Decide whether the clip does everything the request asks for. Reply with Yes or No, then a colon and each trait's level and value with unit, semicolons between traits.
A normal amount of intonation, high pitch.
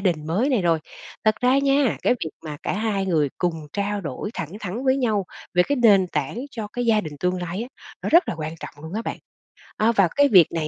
No: wide, 5.8 semitones; high, 200 Hz